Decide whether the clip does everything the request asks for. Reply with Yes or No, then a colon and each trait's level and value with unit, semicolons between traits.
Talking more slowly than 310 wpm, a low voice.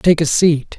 No: fast, 230 wpm; medium, 160 Hz